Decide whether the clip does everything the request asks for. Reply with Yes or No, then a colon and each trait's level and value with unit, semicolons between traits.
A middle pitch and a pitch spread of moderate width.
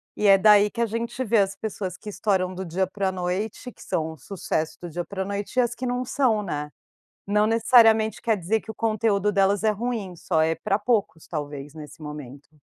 No: high, 200 Hz; average, 3.9 semitones